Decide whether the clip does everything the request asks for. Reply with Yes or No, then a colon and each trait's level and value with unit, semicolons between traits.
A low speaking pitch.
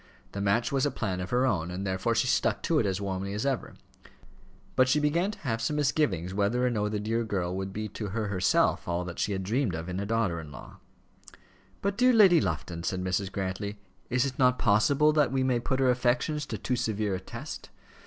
Yes: low, 110 Hz